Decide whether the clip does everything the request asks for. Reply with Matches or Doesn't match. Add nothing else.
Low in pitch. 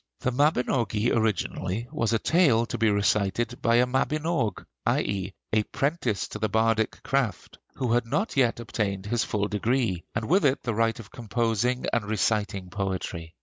Matches